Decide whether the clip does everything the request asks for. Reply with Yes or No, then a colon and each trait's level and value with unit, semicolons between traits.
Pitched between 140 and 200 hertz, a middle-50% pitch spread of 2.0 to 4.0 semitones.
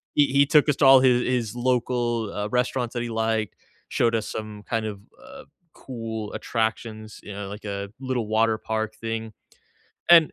No: low, 115 Hz; narrow, 2.4 semitones